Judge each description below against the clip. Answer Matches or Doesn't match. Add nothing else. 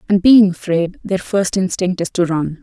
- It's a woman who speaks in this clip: Matches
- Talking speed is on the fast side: Doesn't match